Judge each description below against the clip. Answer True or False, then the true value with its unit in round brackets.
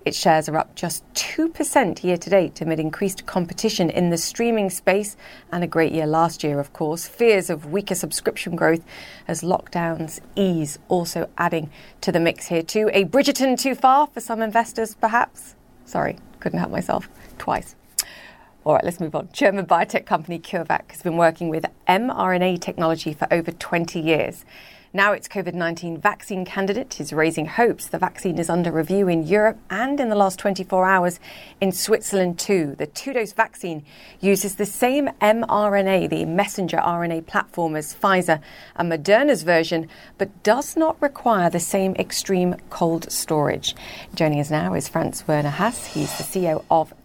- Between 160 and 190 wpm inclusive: True (170 wpm)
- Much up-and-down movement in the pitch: False (3.9 semitones)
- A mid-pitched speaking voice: True (180 Hz)